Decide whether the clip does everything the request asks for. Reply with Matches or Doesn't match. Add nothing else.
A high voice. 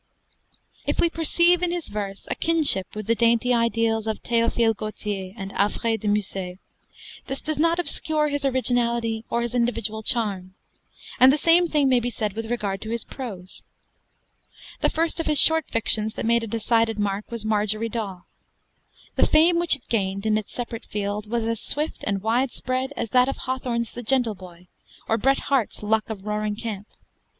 Matches